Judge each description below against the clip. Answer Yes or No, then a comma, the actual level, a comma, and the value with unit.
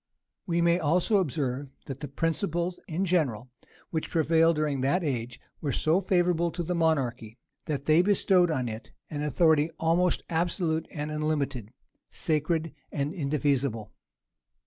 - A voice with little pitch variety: No, average, 3.6 semitones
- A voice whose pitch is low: No, medium, 155 Hz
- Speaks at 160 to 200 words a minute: No, slow, 135 wpm